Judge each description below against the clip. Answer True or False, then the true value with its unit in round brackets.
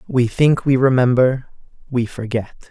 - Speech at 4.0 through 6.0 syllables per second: True (4.5 syllables/s)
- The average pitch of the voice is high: False (125 Hz)